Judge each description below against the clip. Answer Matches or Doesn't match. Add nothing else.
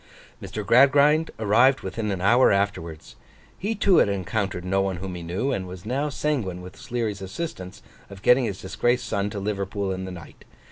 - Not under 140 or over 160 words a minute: Doesn't match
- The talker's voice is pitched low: Matches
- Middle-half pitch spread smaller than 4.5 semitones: Doesn't match